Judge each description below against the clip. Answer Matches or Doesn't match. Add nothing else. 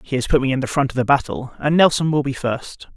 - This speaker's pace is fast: Matches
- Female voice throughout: Doesn't match